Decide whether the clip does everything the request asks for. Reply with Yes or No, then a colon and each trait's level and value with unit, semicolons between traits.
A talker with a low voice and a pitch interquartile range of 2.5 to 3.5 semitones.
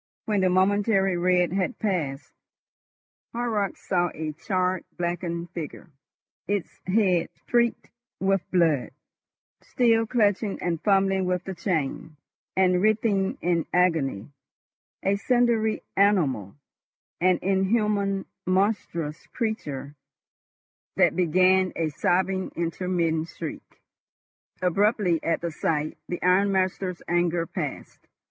No: medium, 185 Hz; average, 2.9 semitones